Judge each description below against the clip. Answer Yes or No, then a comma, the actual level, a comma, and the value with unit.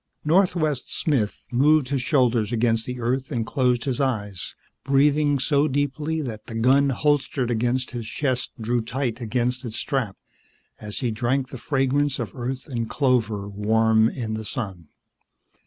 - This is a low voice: Yes, low, 125 Hz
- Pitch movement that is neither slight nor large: Yes, average, 3.6 semitones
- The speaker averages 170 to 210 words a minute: No, average, 155 wpm